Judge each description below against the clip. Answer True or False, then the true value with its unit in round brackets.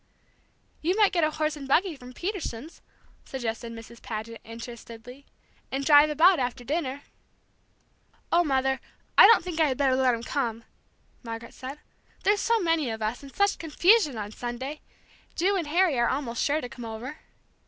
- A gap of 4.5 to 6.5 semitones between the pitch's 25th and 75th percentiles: True (5.5 semitones)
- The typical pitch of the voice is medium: False (275 Hz)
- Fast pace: False (170 wpm)